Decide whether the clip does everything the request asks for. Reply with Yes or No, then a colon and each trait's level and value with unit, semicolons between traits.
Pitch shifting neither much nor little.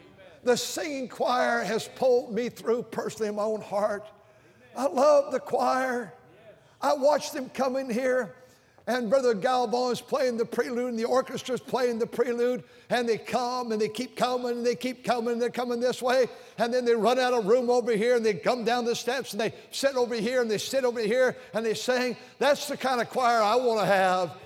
No: narrow, 1.9 semitones